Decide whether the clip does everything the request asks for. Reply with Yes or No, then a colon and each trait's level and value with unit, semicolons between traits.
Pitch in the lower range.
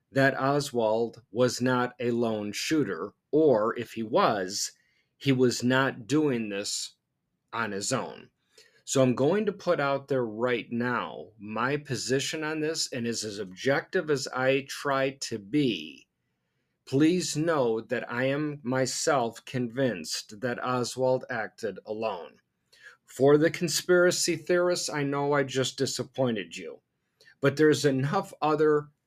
Yes: low, 130 Hz